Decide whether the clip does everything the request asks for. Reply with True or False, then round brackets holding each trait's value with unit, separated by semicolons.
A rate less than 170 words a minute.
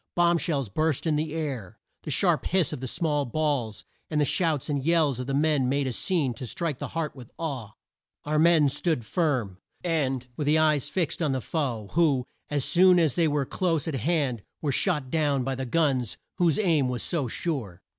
False (205 wpm)